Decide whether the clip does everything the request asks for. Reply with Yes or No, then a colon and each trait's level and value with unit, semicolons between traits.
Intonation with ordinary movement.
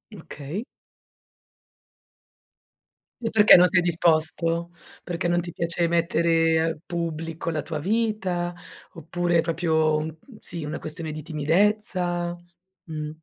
No: narrow, 1.7 semitones